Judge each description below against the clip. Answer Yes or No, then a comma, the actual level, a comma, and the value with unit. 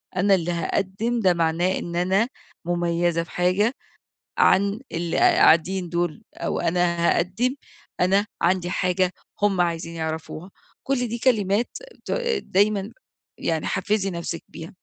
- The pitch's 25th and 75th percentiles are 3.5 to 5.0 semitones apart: No, average, 2.8 semitones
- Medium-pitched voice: Yes, medium, 180 Hz